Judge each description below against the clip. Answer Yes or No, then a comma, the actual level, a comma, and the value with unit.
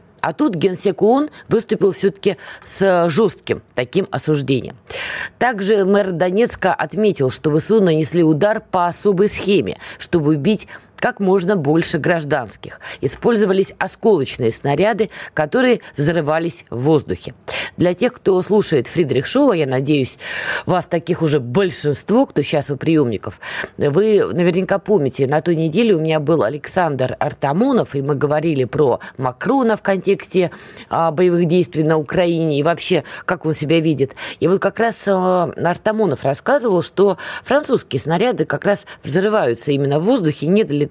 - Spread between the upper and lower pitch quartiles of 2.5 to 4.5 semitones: No, average, 5.0 semitones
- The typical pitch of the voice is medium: Yes, medium, 175 Hz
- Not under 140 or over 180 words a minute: Yes, average, 145 wpm